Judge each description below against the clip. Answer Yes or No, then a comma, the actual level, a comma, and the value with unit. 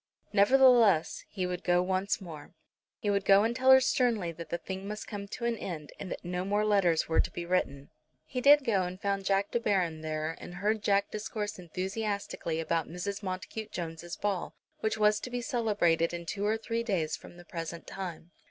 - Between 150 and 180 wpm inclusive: No, fast, 205 wpm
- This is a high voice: Yes, high, 195 Hz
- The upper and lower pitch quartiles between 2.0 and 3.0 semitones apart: No, average, 3.6 semitones